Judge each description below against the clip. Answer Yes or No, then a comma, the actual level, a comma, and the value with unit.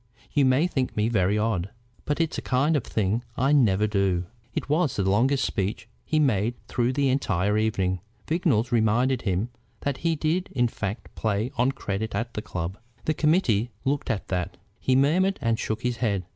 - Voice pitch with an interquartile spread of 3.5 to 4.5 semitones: No, average, 5.2 semitones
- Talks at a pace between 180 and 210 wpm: Yes, average, 185 wpm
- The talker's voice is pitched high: No, low, 115 Hz